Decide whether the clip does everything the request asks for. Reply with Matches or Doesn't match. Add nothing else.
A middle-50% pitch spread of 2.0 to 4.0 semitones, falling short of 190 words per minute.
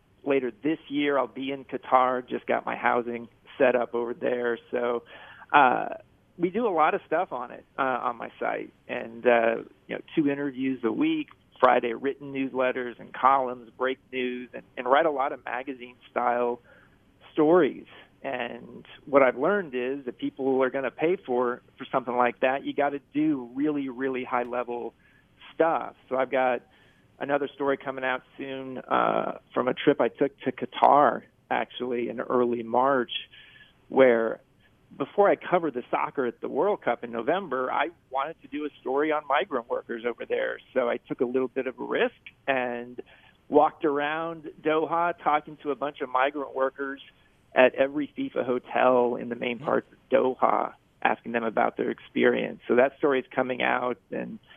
Matches